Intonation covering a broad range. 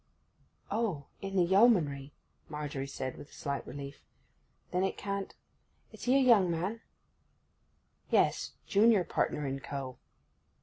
Yes: wide, 6.1 semitones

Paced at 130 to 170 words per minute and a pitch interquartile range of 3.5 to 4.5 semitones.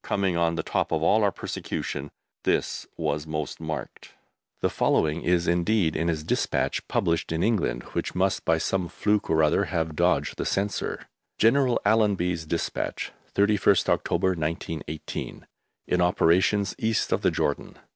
Yes: average, 150 wpm; average, 4.0 semitones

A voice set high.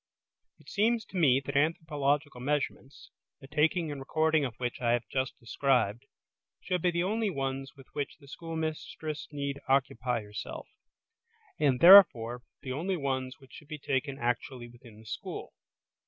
No: medium, 140 Hz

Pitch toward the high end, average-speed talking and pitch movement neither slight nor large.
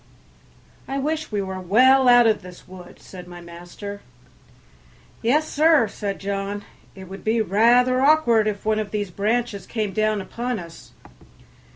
Yes: high, 215 Hz; average, 155 wpm; average, 3.8 semitones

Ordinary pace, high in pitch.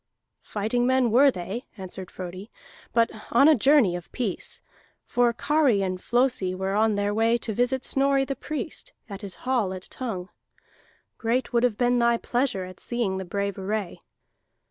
Yes: average, 165 wpm; high, 230 Hz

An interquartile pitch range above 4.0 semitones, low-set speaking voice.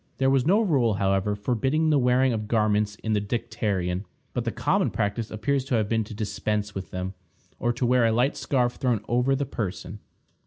No: average, 3.6 semitones; low, 115 Hz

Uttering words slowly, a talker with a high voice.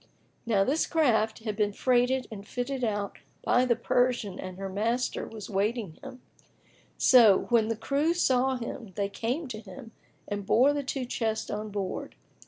No: average, 170 wpm; high, 230 Hz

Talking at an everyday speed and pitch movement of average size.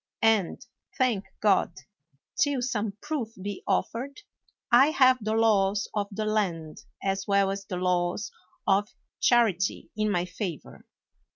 No: slow, 130 wpm; average, 3.0 semitones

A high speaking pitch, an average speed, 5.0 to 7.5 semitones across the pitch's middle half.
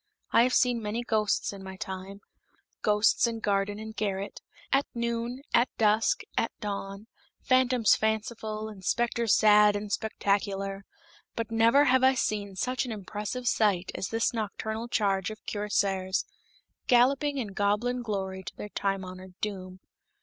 No: high, 210 Hz; average, 150 wpm; average, 3.0 semitones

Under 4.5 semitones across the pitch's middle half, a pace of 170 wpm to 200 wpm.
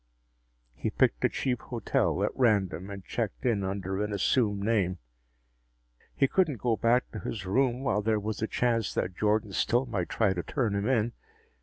Yes: average, 3.3 semitones; average, 180 wpm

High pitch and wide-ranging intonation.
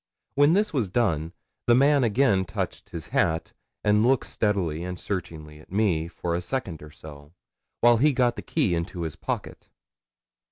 No: very low, 95 Hz; wide, 6.9 semitones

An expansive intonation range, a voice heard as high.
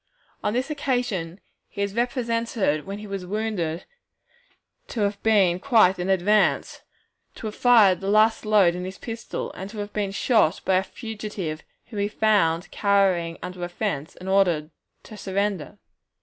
No: average, 3.1 semitones; high, 200 Hz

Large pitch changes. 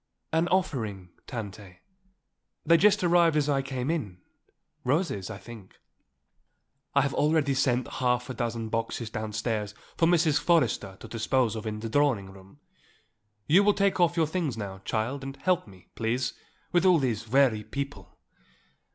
Yes: wide, 6.5 semitones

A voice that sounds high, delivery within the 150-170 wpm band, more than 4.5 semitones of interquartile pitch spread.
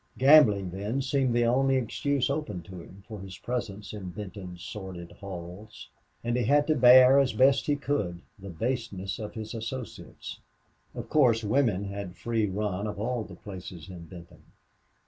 No: low, 105 Hz; average, 165 wpm; average, 5.1 semitones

